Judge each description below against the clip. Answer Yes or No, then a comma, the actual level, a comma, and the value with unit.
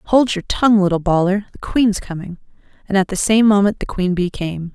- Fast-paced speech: Yes, fast, 215 wpm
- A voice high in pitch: Yes, high, 195 Hz